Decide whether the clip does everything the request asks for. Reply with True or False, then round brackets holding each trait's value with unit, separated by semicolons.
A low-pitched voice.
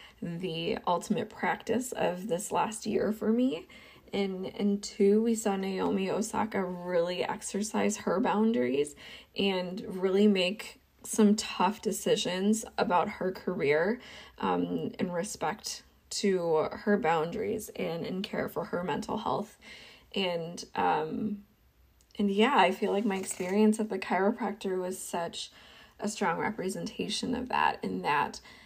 False (205 Hz)